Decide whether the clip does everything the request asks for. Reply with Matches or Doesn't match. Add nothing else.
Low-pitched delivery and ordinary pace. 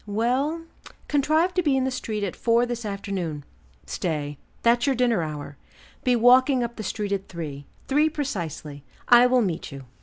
Doesn't match